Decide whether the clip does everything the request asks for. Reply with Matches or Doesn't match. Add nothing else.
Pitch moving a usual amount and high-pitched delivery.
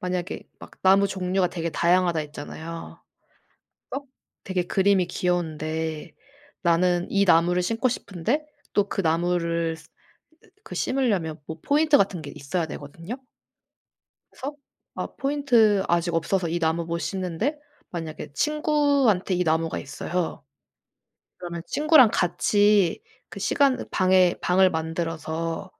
Doesn't match